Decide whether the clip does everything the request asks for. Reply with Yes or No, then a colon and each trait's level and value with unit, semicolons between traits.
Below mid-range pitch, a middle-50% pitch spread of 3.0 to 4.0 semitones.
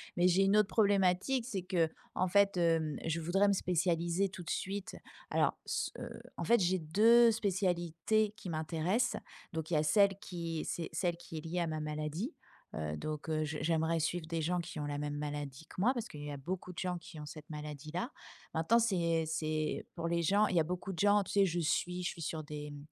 No: medium, 170 Hz; average, 3.7 semitones